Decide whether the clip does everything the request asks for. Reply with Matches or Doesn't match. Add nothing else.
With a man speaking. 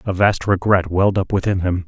Matches